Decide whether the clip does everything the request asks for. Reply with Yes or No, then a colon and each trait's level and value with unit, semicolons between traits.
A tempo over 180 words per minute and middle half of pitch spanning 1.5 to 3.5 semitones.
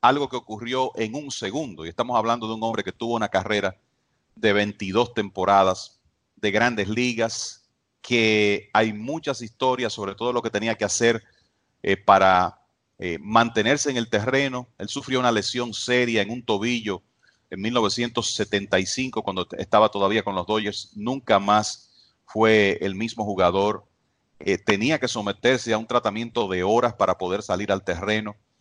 No: average, 160 wpm; average, 2.8 semitones